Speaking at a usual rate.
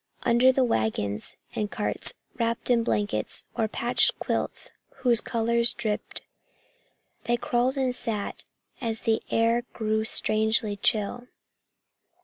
No: slow, 120 wpm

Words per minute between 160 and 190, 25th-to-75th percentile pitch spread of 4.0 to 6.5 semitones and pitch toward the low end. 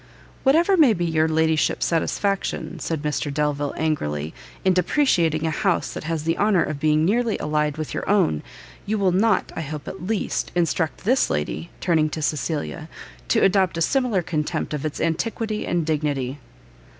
No: average, 170 wpm; average, 4.5 semitones; medium, 160 Hz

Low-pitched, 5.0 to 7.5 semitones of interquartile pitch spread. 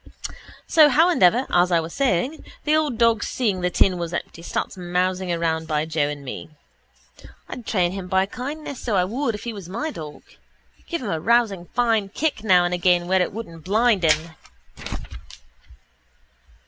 No: high, 190 Hz; wide, 5.4 semitones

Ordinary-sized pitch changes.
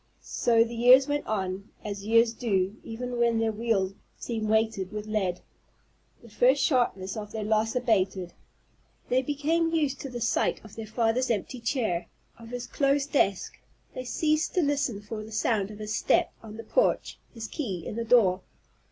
Yes: average, 3.2 semitones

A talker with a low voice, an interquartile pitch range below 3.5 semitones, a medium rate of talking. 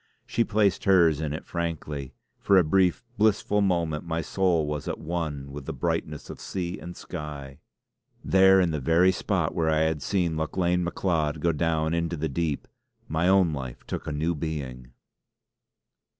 Yes: very low, 80 Hz; average, 2.9 semitones; average, 170 wpm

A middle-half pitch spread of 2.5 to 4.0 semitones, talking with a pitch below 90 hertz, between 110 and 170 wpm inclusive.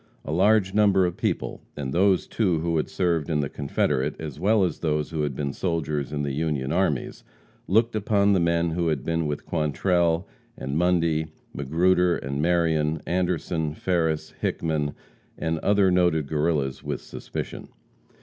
Yes: average, 3.1 semitones; very low, 80 Hz; average, 160 wpm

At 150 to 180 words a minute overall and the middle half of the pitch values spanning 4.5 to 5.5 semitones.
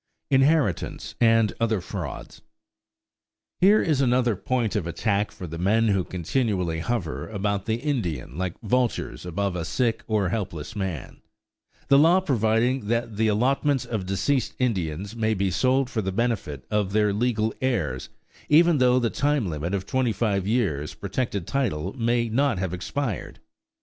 Yes: average, 155 wpm; average, 5.0 semitones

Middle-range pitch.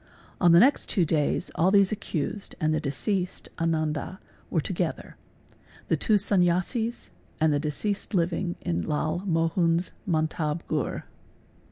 Yes: medium, 170 Hz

